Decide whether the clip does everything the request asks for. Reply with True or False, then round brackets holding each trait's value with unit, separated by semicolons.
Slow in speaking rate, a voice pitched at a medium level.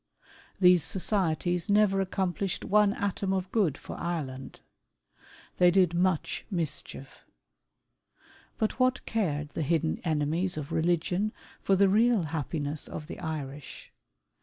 True (120 wpm; 175 Hz)